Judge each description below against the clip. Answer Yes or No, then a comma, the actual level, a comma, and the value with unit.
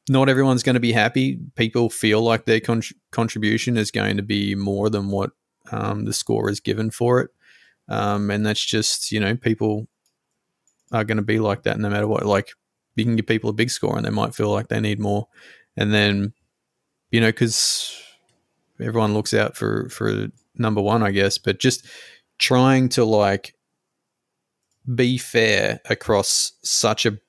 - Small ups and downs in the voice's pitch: Yes, narrow, 2.1 semitones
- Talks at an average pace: Yes, average, 180 wpm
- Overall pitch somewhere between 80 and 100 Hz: No, low, 110 Hz